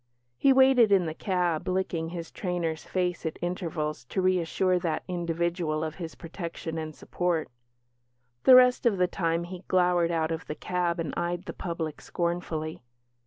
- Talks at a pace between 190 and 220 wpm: No, average, 165 wpm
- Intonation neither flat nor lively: No, narrow, 2.0 semitones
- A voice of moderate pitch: Yes, medium, 175 Hz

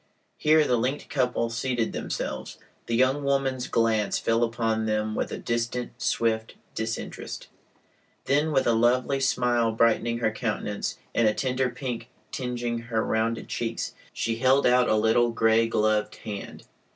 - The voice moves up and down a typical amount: No, narrow, 2.1 semitones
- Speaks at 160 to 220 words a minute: No, average, 150 wpm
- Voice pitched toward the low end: Yes, low, 115 Hz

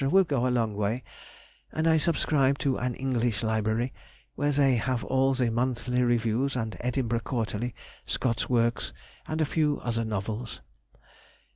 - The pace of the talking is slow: No, average, 150 wpm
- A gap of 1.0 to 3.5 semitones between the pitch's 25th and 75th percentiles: Yes, average, 2.8 semitones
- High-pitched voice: No, low, 125 Hz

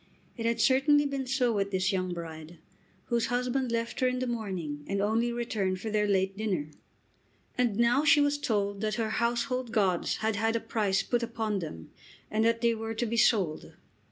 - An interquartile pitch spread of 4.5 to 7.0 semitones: No, average, 3.4 semitones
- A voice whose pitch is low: No, high, 225 Hz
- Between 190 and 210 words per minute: Yes, average, 195 wpm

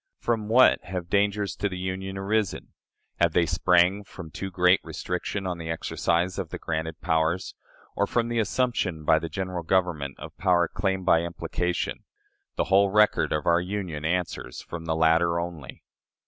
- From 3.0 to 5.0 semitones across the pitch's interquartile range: No, narrow, 2.6 semitones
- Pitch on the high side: No, very low, 90 Hz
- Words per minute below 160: No, average, 170 wpm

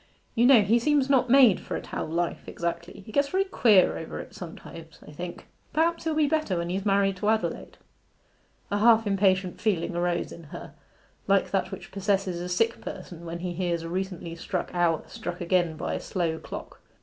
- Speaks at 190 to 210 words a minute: Yes, average, 195 wpm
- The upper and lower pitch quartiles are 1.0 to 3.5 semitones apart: No, average, 4.5 semitones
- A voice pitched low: No, medium, 185 Hz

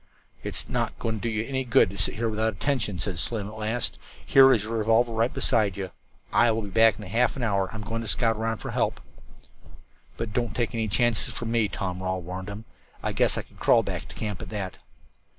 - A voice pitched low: Yes, low, 110 Hz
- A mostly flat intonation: Yes, narrow, 2.3 semitones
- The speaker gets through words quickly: Yes, fast, 230 wpm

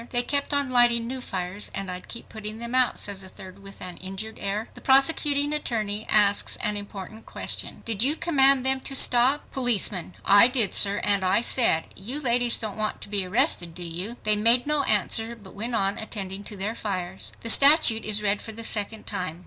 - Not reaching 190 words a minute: No, fast, 205 wpm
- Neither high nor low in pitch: No, high, 215 Hz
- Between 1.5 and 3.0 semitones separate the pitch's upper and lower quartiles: No, average, 3.7 semitones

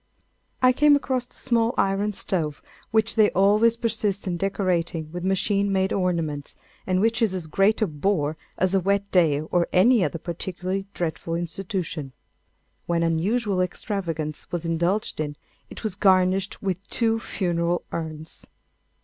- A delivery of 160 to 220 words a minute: No, average, 150 wpm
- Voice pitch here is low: No, medium, 185 Hz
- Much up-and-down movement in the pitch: No, average, 3.5 semitones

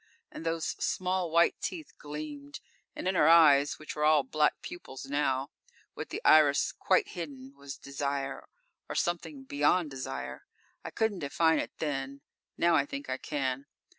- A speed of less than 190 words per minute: Yes, average, 160 wpm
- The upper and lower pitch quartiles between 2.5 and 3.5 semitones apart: Yes, average, 3.2 semitones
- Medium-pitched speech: Yes, medium, 150 Hz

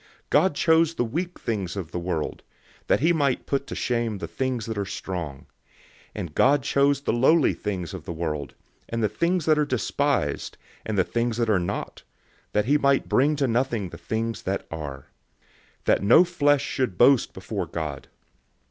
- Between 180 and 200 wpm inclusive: Yes, average, 190 wpm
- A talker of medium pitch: No, low, 120 Hz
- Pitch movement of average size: No, wide, 7.0 semitones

